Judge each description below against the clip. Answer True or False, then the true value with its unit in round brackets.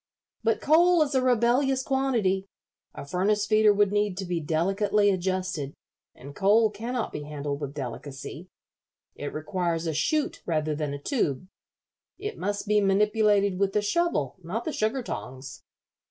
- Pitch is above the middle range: True (200 Hz)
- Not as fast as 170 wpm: True (155 wpm)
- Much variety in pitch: True (6.2 semitones)